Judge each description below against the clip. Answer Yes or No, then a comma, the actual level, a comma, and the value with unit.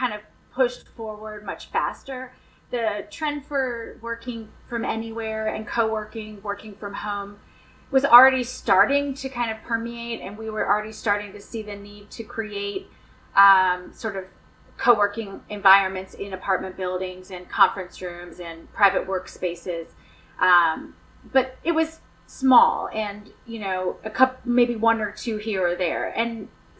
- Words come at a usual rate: Yes, average, 150 wpm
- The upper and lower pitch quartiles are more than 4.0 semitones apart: No, average, 3.3 semitones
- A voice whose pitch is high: Yes, high, 215 Hz